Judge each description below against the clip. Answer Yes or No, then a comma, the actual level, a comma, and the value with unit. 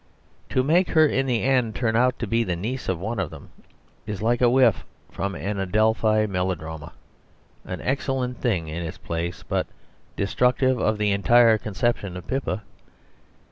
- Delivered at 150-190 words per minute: Yes, average, 170 wpm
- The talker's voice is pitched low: Yes, low, 110 Hz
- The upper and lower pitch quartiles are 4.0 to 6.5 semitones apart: Yes, average, 4.6 semitones